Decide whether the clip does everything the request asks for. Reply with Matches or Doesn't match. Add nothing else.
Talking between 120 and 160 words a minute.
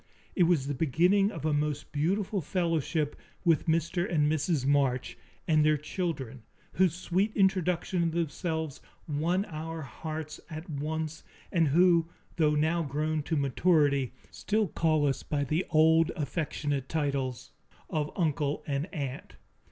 Matches